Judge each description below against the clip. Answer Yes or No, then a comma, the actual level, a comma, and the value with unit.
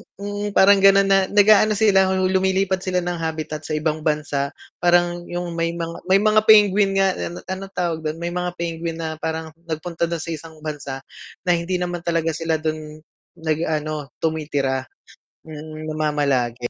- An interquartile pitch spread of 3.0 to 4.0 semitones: Yes, average, 3.3 semitones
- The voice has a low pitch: No, medium, 165 Hz